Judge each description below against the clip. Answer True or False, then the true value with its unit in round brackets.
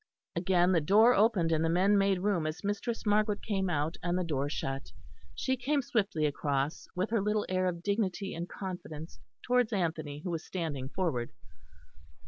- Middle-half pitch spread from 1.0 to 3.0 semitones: False (4.4 semitones)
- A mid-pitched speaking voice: True (180 Hz)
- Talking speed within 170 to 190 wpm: True (175 wpm)